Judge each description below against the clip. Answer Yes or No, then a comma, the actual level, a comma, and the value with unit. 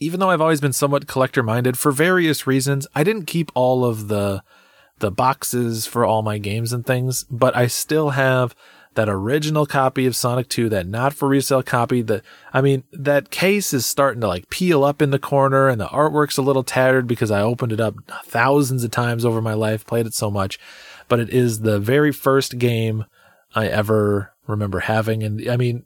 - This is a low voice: Yes, low, 125 Hz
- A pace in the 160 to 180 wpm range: No, fast, 205 wpm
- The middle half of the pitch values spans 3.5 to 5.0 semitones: Yes, average, 3.9 semitones